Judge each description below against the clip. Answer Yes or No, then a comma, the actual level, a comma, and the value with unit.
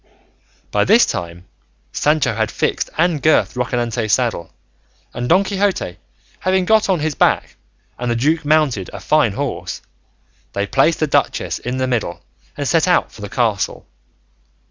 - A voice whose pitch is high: No, low, 130 Hz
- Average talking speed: Yes, average, 155 wpm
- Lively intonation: Yes, wide, 6.1 semitones